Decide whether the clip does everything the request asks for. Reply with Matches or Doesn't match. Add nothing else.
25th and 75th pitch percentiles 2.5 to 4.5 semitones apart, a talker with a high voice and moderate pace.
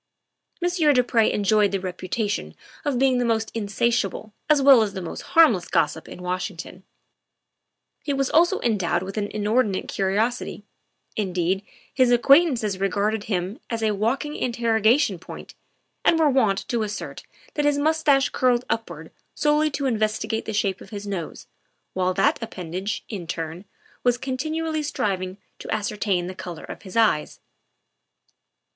Doesn't match